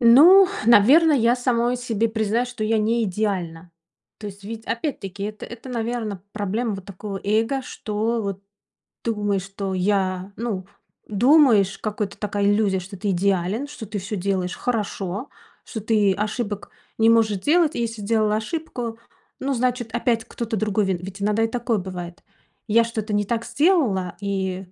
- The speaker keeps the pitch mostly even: No, average, 3.0 semitones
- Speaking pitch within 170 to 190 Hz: No, high, 215 Hz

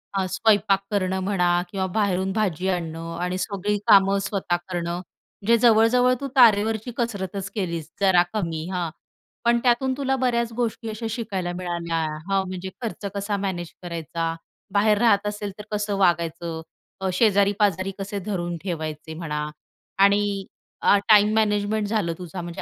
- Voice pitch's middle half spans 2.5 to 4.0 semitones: Yes, average, 3.3 semitones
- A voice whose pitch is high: Yes, high, 195 Hz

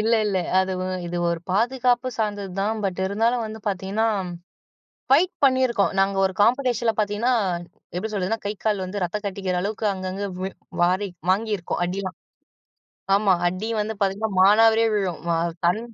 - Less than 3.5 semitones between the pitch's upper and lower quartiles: Yes, average, 2.9 semitones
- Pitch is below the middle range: No, high, 205 Hz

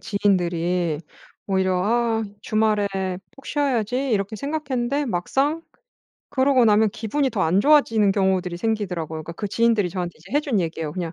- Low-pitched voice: No, high, 210 Hz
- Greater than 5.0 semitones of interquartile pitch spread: Yes, wide, 5.6 semitones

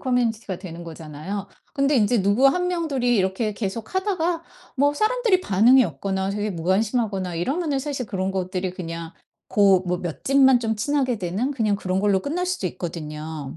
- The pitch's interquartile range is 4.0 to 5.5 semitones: No, wide, 6.7 semitones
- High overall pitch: Yes, high, 210 Hz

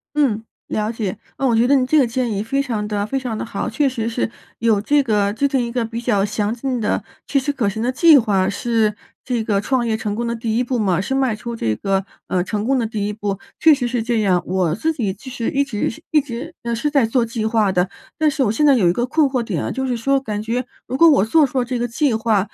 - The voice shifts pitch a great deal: No, average, 3.8 semitones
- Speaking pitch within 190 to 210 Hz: No, high, 230 Hz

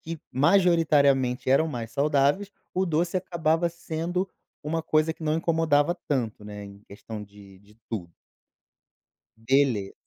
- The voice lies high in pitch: No, medium, 145 Hz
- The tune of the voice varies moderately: No, wide, 6.5 semitones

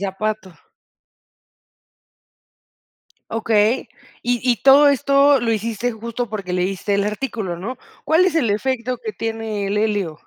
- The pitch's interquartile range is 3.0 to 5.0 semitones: Yes, average, 3.8 semitones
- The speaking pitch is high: Yes, high, 225 Hz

